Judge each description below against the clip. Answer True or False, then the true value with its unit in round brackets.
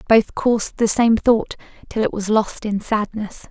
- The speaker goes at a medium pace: True (190 wpm)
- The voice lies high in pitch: True (215 Hz)